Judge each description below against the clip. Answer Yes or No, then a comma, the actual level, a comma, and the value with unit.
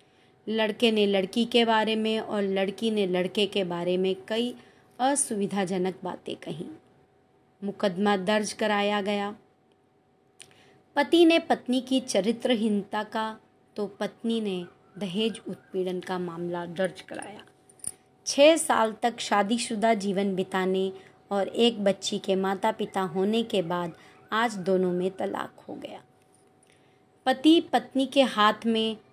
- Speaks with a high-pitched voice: Yes, high, 205 Hz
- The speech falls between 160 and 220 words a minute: No, average, 130 wpm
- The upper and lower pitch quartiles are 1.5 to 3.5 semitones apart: Yes, average, 3.1 semitones